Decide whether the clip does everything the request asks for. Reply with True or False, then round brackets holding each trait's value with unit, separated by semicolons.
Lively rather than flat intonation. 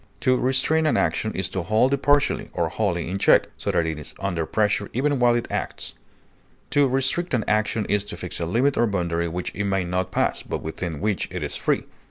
True (6.4 semitones)